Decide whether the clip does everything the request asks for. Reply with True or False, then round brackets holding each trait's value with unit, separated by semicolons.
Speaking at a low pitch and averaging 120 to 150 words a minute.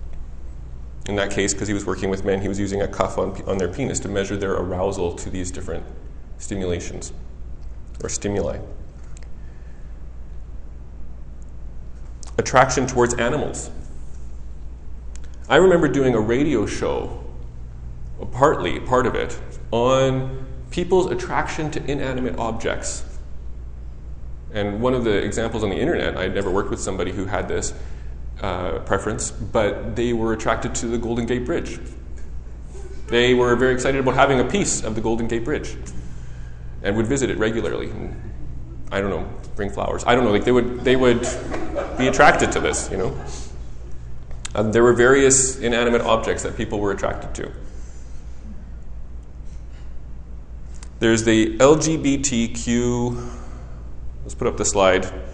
True (75 Hz; 140 wpm)